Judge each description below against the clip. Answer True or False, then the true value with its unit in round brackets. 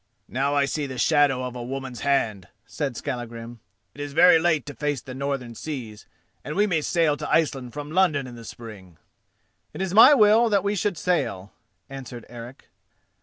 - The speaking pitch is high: False (140 Hz)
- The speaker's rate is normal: True (185 wpm)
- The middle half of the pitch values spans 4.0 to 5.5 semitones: True (4.8 semitones)